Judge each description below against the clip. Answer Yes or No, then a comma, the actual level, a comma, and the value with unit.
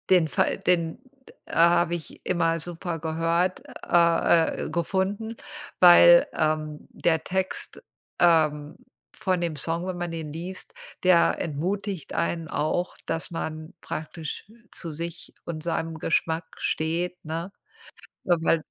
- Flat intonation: Yes, narrow, 1.6 semitones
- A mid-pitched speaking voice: Yes, medium, 170 Hz